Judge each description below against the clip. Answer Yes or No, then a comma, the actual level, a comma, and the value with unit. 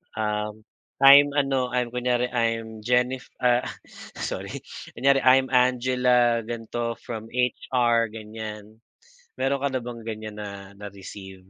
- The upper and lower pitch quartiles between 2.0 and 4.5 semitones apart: Yes, narrow, 2.6 semitones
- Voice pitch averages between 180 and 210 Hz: No, low, 120 Hz